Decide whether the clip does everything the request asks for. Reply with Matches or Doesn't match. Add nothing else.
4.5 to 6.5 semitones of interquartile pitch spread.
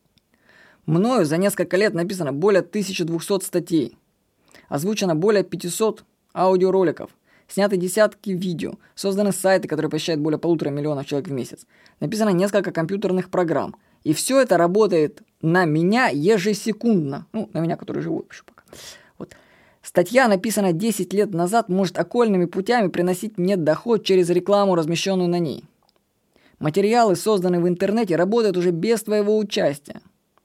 Doesn't match